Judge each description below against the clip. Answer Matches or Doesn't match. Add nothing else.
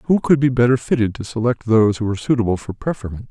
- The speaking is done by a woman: Doesn't match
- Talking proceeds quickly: Matches